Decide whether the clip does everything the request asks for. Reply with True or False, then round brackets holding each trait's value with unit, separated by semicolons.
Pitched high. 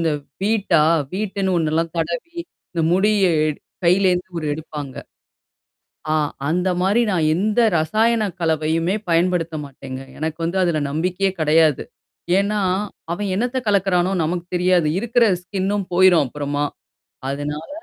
False (175 Hz)